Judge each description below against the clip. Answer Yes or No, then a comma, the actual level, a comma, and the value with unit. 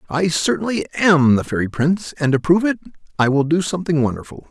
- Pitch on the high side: No, medium, 160 Hz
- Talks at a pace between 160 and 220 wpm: Yes, average, 200 wpm